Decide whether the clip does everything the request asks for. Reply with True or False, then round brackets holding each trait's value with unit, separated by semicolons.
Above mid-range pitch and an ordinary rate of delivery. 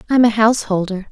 True (215 Hz; 160 wpm)